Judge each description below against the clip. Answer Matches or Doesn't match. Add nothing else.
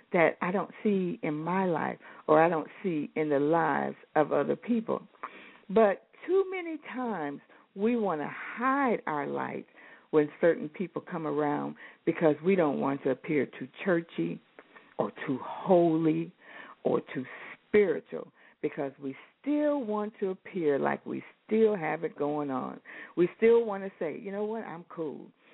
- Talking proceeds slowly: Doesn't match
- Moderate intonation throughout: Doesn't match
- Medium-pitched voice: Matches